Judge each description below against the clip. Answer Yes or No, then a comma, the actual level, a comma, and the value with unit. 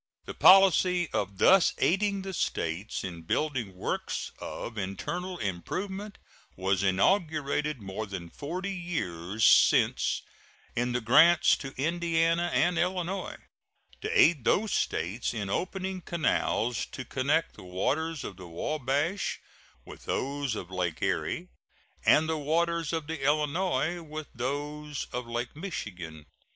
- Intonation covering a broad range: Yes, wide, 8.7 semitones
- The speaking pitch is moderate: Yes, medium, 150 Hz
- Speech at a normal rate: No, slow, 130 wpm